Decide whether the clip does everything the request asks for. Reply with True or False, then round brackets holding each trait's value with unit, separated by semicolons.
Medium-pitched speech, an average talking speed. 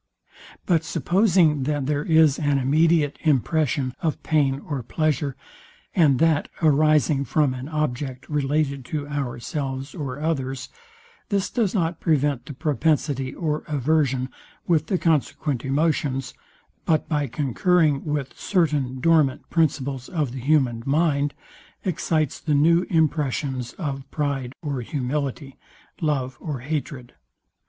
False (145 Hz; 125 wpm)